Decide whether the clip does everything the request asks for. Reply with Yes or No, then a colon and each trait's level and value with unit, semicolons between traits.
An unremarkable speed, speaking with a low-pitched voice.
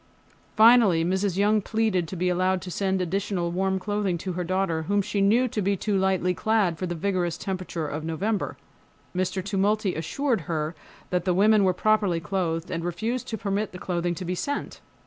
No: average, 190 wpm; high, 190 Hz